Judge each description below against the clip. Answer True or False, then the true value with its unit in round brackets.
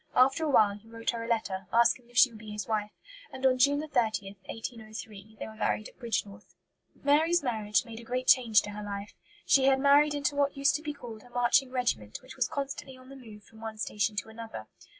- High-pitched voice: True (235 Hz)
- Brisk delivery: True (230 wpm)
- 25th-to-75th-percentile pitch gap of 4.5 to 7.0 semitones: False (3.8 semitones)